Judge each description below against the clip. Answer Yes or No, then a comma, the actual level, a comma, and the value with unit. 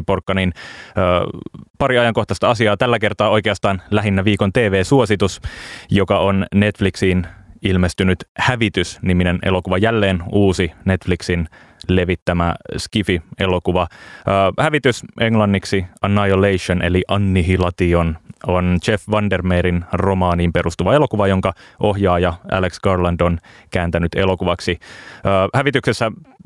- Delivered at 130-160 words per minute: No, average, 100 wpm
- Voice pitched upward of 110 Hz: No, very low, 95 Hz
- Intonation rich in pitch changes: No, narrow, 2.6 semitones